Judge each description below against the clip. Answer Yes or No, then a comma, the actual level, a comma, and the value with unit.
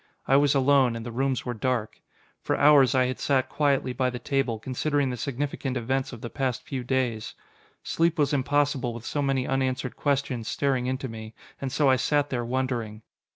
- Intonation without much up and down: Yes, narrow, 2.2 semitones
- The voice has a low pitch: Yes, low, 130 Hz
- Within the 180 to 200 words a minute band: Yes, average, 195 wpm